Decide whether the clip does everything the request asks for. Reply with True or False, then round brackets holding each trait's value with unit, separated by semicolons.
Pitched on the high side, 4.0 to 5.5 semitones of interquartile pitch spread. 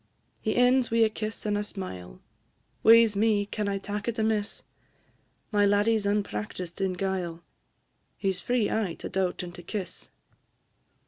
False (205 Hz; 2.7 semitones)